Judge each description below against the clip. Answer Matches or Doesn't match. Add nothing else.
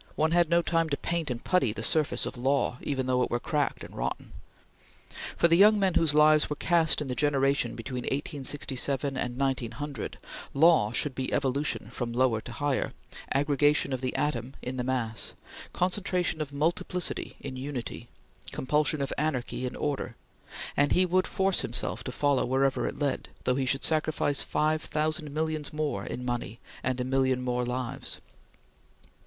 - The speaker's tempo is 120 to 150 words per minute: Doesn't match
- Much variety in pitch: Doesn't match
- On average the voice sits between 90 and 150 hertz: Matches